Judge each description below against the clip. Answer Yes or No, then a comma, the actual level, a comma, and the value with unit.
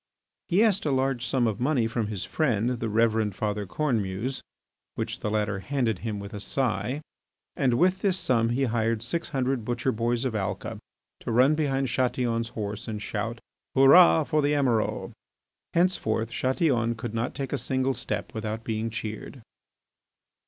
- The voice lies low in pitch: Yes, low, 120 Hz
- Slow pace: No, average, 165 wpm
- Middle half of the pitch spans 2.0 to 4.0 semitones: Yes, average, 3.6 semitones